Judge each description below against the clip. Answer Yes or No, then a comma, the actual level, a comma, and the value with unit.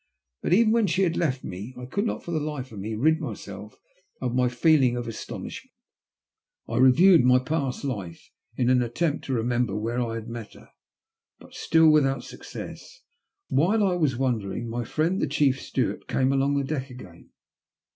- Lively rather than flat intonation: No, average, 4.7 semitones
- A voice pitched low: Yes, low, 130 Hz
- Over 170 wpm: Yes, average, 185 wpm